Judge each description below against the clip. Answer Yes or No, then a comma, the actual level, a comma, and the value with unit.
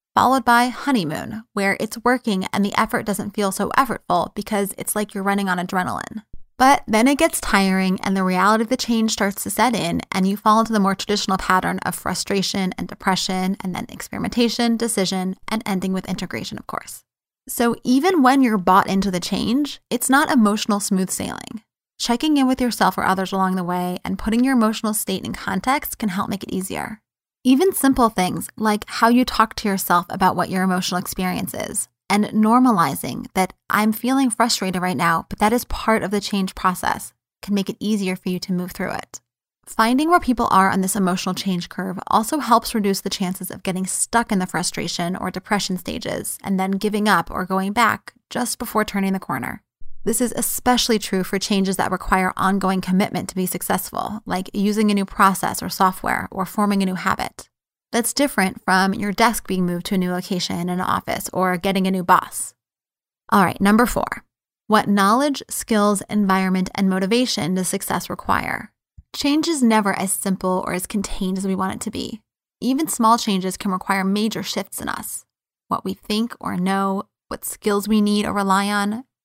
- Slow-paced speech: No, average, 195 wpm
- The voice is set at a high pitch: Yes, high, 200 Hz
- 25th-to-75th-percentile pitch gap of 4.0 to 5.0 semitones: No, average, 3.3 semitones